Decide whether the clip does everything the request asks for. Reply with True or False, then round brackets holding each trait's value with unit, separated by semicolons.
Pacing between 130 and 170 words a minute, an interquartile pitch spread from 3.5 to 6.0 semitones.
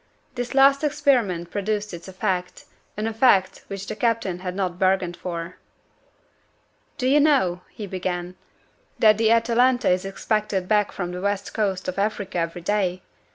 True (155 wpm; 3.8 semitones)